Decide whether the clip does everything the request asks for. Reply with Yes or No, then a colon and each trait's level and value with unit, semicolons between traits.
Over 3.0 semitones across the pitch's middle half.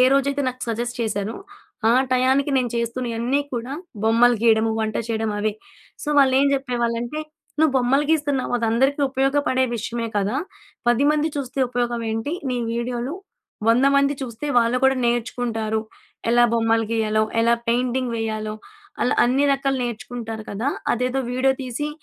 No: average, 2.7 semitones